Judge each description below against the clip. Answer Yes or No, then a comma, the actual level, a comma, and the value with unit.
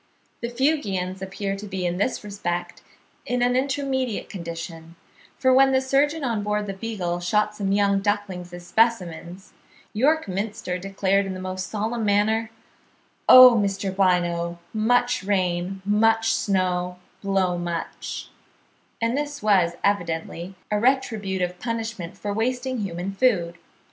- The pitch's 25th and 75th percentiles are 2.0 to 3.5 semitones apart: No, average, 4.0 semitones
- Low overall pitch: No, high, 200 Hz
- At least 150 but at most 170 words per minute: No, slow, 135 wpm